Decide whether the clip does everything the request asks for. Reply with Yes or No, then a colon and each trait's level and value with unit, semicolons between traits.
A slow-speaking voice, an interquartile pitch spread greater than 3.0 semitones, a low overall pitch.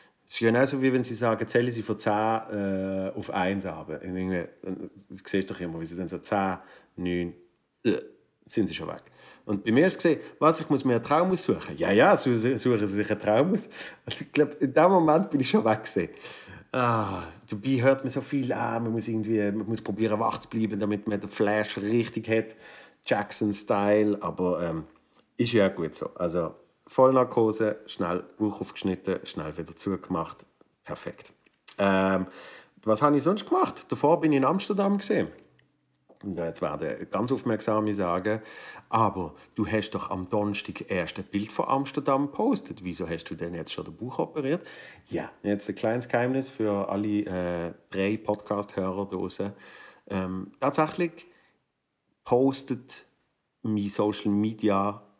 No: average, 170 wpm; average, 4.1 semitones; low, 105 Hz